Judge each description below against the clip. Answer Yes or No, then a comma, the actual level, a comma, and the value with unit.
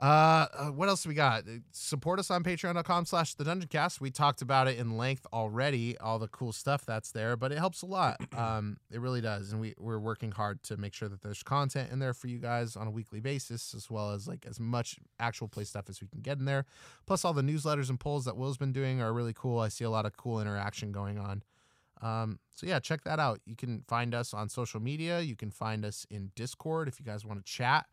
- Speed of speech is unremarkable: No, fast, 245 wpm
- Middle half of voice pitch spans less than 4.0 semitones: No, average, 4.7 semitones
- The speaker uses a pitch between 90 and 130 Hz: Yes, low, 120 Hz